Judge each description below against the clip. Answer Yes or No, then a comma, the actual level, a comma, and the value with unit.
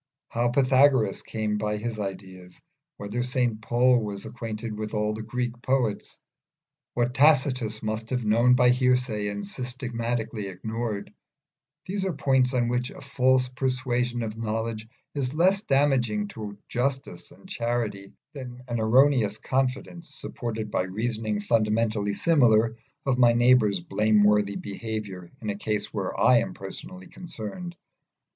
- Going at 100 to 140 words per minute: Yes, slow, 135 wpm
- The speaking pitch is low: Yes, low, 115 Hz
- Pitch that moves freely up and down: No, average, 3.1 semitones